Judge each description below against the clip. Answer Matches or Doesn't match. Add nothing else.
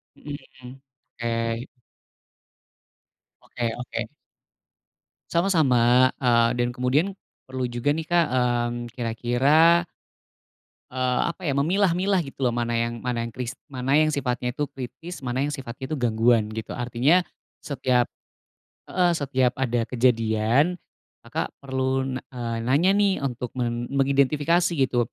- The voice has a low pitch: Matches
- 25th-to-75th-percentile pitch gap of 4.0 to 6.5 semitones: Doesn't match